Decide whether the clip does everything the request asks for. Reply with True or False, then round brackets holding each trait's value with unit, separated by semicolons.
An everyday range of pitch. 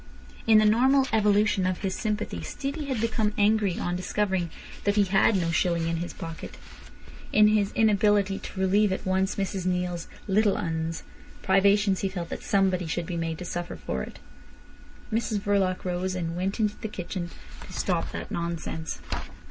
True (3.1 semitones)